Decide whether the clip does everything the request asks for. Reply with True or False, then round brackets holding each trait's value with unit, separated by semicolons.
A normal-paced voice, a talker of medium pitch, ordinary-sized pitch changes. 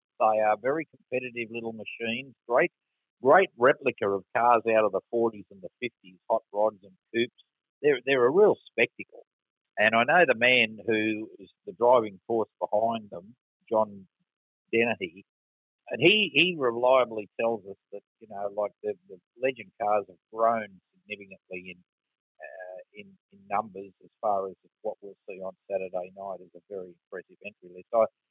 False (165 wpm; 110 Hz; 3.4 semitones)